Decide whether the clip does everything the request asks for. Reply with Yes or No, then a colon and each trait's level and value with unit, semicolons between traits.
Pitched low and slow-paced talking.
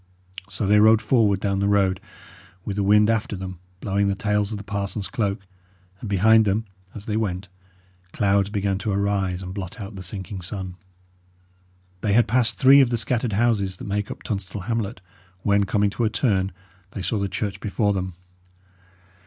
No: low, 100 Hz; average, 185 wpm